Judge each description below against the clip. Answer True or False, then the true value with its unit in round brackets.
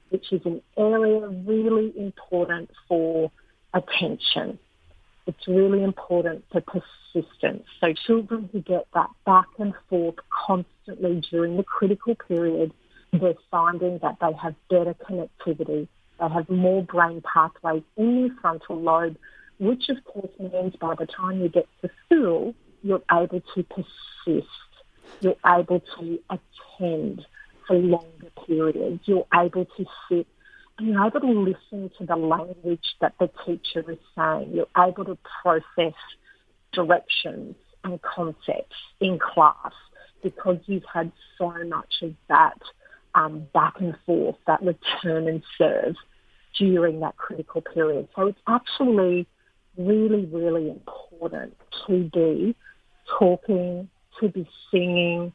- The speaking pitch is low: False (180 Hz)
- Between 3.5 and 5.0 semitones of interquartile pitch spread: False (2.7 semitones)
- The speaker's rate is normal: False (130 wpm)